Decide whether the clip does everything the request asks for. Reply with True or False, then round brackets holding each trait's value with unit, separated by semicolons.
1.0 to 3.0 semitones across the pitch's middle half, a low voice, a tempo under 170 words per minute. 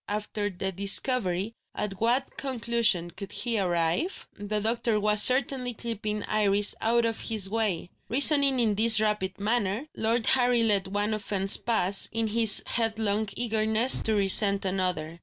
False (2.7 semitones; 215 Hz; 145 wpm)